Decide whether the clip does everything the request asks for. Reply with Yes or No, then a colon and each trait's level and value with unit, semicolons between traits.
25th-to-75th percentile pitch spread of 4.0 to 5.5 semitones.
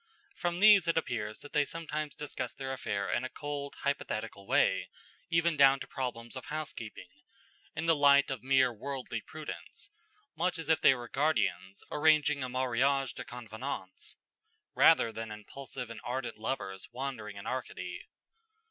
Yes: average, 4.3 semitones